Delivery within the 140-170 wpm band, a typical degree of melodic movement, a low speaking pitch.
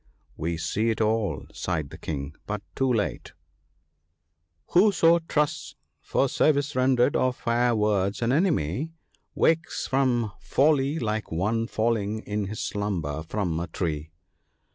No: average, 145 wpm; wide, 7.3 semitones; low, 110 Hz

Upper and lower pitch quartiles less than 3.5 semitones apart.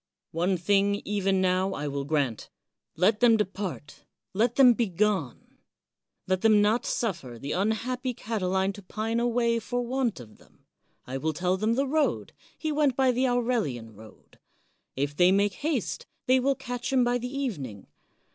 No: wide, 5.4 semitones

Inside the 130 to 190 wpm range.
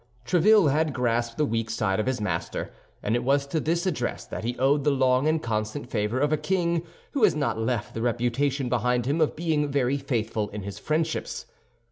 No: fast, 205 wpm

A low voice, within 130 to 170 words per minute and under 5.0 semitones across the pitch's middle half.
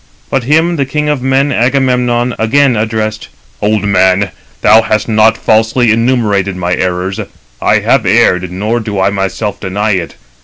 Yes: low, 110 Hz; average, 155 wpm; average, 4.0 semitones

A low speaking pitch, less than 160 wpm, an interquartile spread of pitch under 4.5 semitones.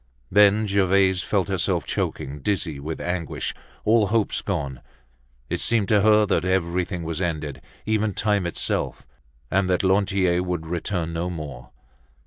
Yes: very low, 90 Hz; average, 140 wpm; average, 3.4 semitones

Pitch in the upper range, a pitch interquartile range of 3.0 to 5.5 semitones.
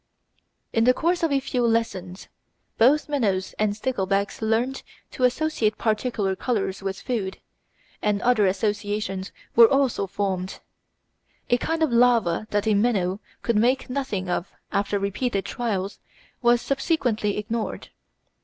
Yes: high, 220 Hz; average, 3.9 semitones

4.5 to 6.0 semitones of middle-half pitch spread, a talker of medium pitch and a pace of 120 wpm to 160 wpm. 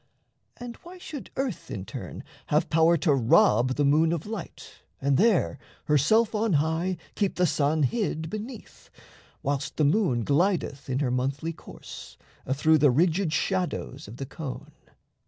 Yes: wide, 5.6 semitones; medium, 160 Hz; average, 155 wpm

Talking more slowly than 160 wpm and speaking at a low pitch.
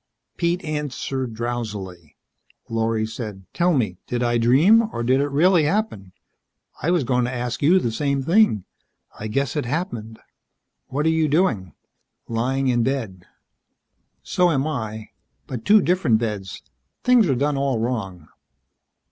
Yes: average, 150 wpm; low, 125 Hz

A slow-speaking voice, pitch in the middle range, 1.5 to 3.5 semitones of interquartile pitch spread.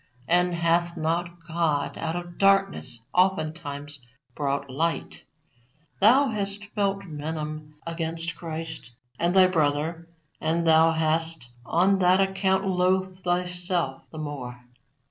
Yes: slow, 115 wpm; medium, 170 Hz; average, 2.9 semitones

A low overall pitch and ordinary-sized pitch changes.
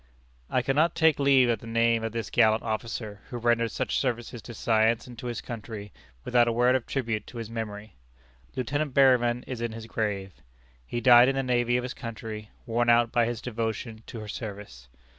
No: low, 115 Hz; narrow, 1.9 semitones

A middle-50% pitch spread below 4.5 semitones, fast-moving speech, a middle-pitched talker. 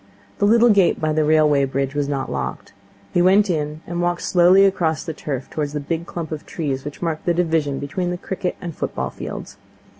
Yes: average, 3.2 semitones; fast, 210 wpm; medium, 160 Hz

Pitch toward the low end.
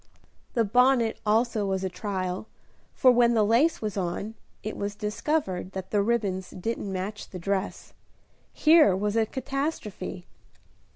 No: high, 210 Hz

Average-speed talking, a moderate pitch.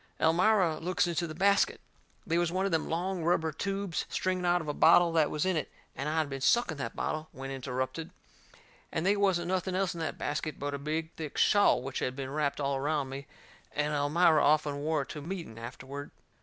No: fast, 215 wpm; medium, 160 Hz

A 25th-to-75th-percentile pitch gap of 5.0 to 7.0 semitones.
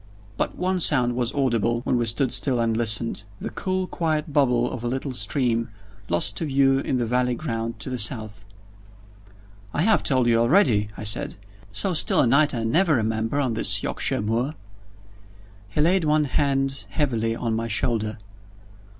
No: average, 4.0 semitones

